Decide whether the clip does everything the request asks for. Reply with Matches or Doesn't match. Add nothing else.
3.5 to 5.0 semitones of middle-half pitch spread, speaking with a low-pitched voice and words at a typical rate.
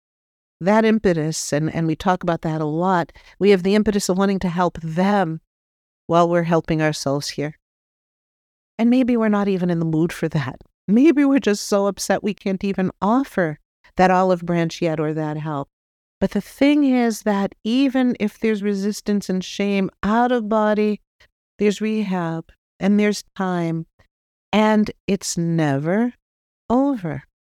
Doesn't match